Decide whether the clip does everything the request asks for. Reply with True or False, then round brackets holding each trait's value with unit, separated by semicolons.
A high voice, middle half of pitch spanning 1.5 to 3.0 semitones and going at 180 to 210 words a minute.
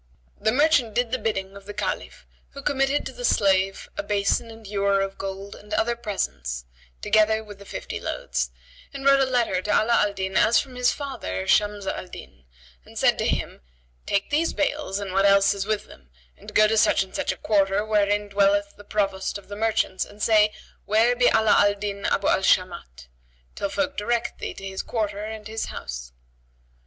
True (205 Hz; 2.4 semitones; 200 wpm)